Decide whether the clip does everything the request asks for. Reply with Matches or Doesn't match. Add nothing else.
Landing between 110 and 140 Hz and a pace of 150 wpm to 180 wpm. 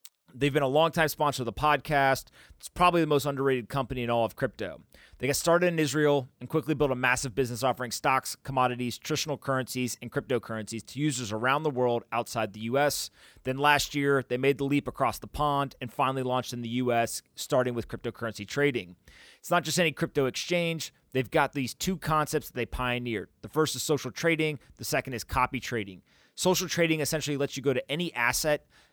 Doesn't match